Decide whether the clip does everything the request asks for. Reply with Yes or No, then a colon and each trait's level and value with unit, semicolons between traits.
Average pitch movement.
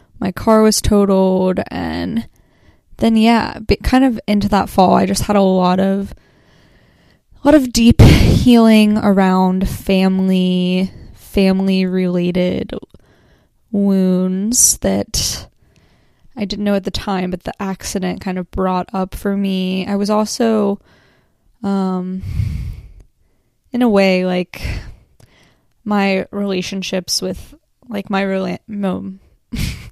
No: narrow, 2.0 semitones